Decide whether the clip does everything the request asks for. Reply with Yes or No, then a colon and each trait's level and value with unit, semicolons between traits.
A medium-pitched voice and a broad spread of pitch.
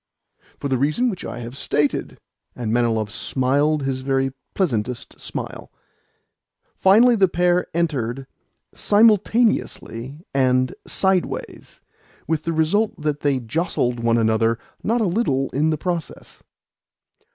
Yes: medium, 145 Hz; wide, 6.1 semitones